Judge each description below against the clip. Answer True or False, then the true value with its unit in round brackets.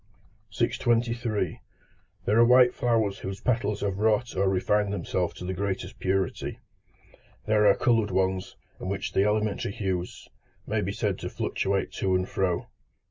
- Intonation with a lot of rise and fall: False (2.9 semitones)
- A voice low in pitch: True (100 Hz)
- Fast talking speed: False (150 wpm)